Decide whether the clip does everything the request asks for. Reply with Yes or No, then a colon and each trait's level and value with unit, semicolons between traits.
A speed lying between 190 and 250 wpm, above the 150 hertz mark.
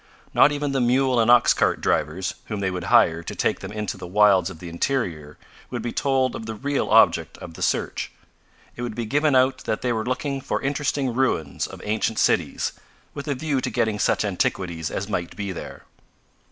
No: fast, 205 wpm; low, 110 Hz